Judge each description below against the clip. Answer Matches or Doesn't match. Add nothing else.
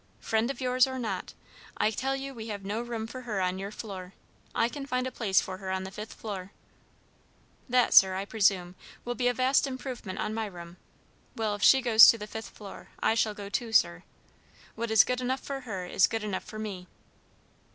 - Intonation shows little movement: Doesn't match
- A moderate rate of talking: Doesn't match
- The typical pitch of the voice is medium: Doesn't match